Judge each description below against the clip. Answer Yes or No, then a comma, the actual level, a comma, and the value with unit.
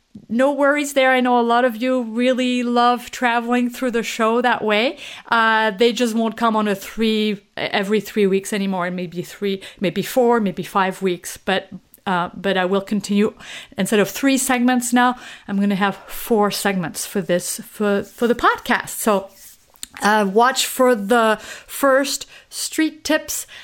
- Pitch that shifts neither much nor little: Yes, average, 3.8 semitones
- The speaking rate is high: No, average, 170 wpm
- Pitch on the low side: No, high, 225 Hz